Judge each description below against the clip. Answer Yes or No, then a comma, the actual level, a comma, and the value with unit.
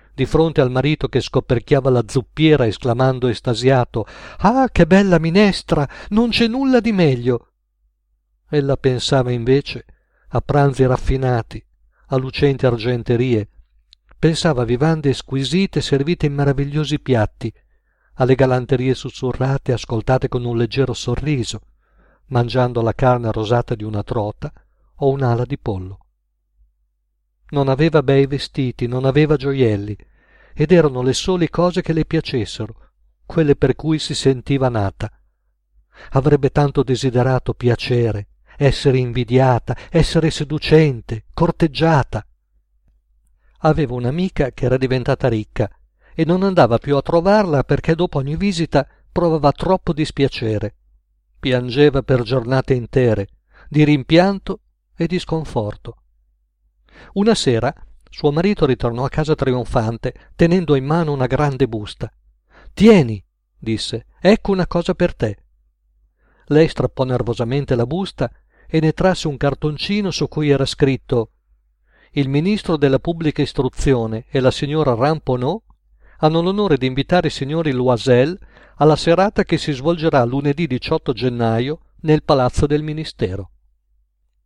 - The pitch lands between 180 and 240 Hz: No, low, 135 Hz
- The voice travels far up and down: No, average, 4.7 semitones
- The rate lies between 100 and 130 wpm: Yes, average, 125 wpm